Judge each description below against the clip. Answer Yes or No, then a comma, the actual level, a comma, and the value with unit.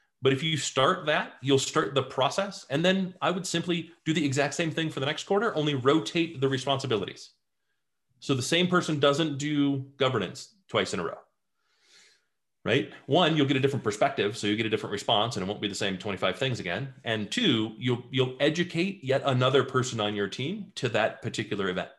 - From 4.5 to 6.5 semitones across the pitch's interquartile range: No, average, 4.0 semitones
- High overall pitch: No, medium, 140 Hz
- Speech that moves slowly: No, fast, 205 wpm